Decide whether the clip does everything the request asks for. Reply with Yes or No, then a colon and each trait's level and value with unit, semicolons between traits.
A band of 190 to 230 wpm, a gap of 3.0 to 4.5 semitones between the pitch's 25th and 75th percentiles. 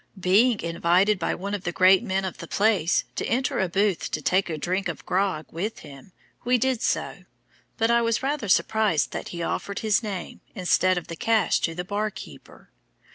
Yes: average, 200 wpm; average, 3.6 semitones